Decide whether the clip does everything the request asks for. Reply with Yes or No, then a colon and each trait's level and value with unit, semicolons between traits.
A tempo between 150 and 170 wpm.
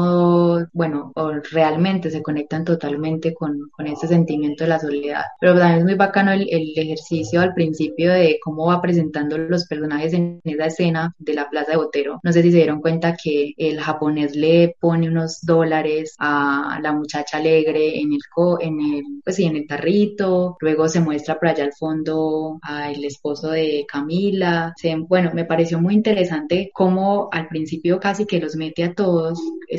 No: average, 185 wpm